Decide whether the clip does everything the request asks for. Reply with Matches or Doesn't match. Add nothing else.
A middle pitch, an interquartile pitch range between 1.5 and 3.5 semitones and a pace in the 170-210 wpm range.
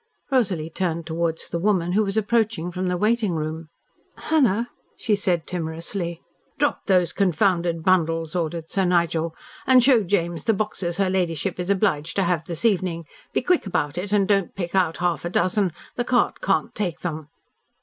Matches